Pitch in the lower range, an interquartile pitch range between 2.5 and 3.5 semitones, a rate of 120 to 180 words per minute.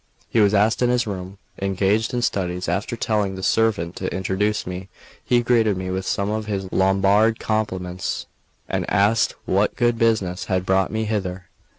Yes: low, 100 Hz; average, 2.8 semitones; average, 170 wpm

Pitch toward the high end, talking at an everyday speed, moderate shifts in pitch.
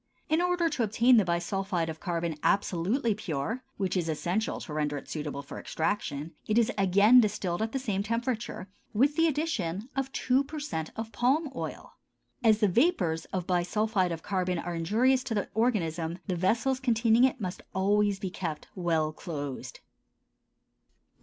No: high, 200 Hz; average, 165 wpm; wide, 5.8 semitones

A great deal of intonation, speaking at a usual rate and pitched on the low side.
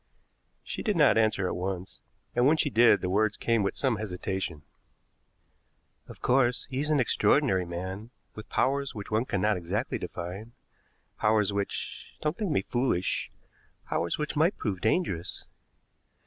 Yes: wide, 5.7 semitones; average, 150 wpm; low, 110 Hz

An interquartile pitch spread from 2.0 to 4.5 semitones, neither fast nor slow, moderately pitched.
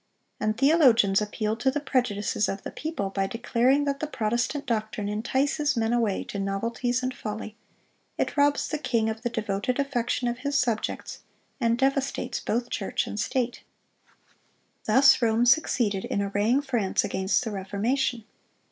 No: average, 4.0 semitones; average, 155 wpm; high, 235 Hz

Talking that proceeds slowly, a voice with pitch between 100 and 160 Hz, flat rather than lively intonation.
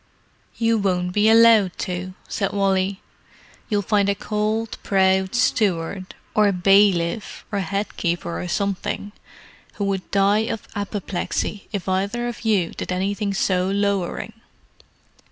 No: slow, 130 wpm; high, 200 Hz; narrow, 2.0 semitones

